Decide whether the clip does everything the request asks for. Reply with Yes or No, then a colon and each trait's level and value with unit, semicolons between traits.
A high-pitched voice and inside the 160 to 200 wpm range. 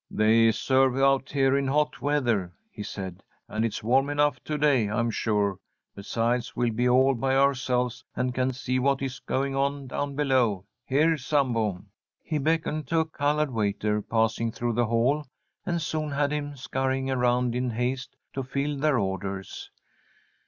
No: low, 130 Hz; average, 165 wpm